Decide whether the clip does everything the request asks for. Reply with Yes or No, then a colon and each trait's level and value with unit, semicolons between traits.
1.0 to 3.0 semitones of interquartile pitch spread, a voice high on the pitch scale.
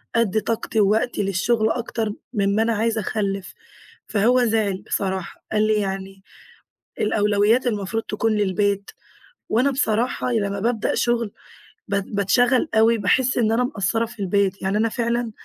Yes: narrow, 2.6 semitones; high, 215 Hz